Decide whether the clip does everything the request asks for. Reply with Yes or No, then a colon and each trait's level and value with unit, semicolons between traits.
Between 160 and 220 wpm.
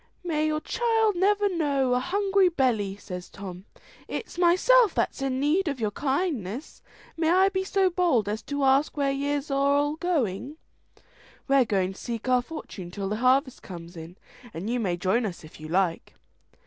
Yes: average, 180 wpm